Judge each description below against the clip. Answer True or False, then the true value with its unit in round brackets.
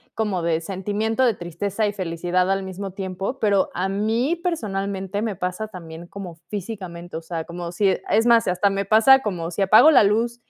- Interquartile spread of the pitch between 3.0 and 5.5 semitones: True (3.3 semitones)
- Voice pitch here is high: True (195 Hz)